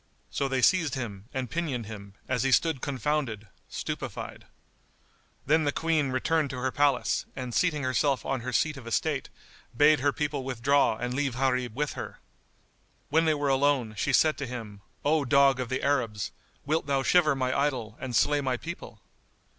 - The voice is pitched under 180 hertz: Yes, low, 135 Hz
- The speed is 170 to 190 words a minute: Yes, average, 180 wpm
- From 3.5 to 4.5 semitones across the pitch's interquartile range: No, average, 2.9 semitones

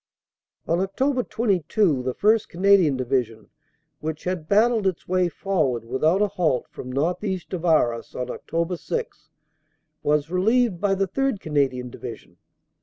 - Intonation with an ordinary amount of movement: No, wide, 5.7 semitones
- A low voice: No, medium, 180 Hz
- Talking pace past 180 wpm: No, average, 140 wpm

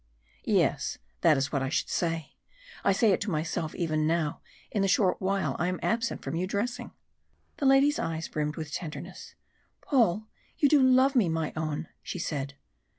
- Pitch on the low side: No, medium, 175 Hz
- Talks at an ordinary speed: Yes, average, 180 wpm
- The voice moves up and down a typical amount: No, wide, 6.3 semitones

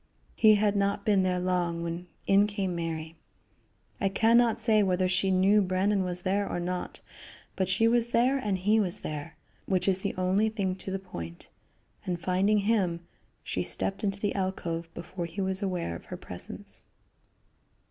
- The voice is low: No, high, 190 Hz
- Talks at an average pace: Yes, average, 180 wpm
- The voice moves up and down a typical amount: No, narrow, 2.3 semitones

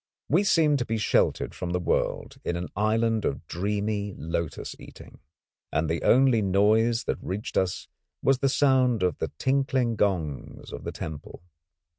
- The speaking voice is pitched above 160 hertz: No, low, 105 Hz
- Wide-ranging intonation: Yes, wide, 5.9 semitones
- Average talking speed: Yes, average, 160 wpm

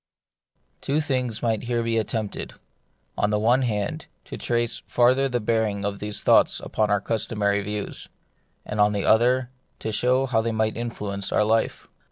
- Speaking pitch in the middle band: No, low, 110 Hz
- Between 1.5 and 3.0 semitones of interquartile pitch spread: Yes, narrow, 2.5 semitones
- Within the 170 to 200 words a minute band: Yes, average, 175 wpm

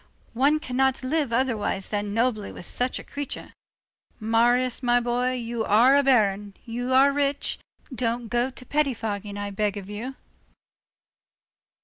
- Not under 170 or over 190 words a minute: No, average, 140 wpm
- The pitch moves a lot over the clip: No, average, 3.4 semitones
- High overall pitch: Yes, high, 240 Hz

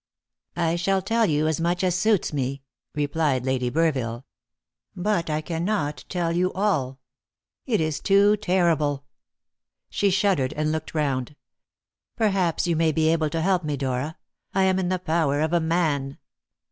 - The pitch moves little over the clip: No, average, 4.1 semitones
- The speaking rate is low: No, average, 160 wpm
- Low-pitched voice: No, medium, 160 Hz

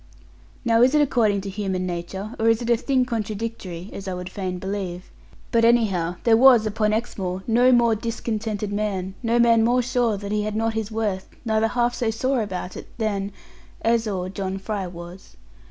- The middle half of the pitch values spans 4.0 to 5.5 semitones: No, average, 3.2 semitones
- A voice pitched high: Yes, high, 215 Hz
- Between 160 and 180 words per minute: No, average, 190 wpm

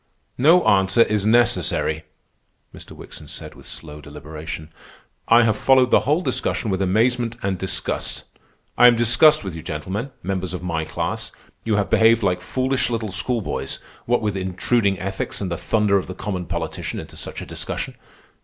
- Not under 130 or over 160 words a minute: No, average, 170 wpm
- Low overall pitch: Yes, low, 100 Hz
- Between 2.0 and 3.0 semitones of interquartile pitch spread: No, average, 4.6 semitones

